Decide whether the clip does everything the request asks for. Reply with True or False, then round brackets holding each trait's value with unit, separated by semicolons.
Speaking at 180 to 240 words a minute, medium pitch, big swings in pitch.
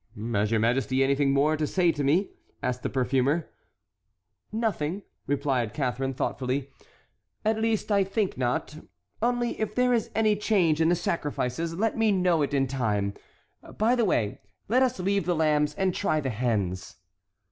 False (165 wpm; 155 Hz; 7.4 semitones)